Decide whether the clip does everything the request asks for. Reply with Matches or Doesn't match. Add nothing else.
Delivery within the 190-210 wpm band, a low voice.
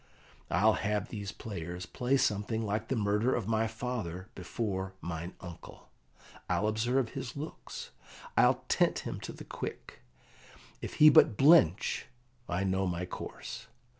Doesn't match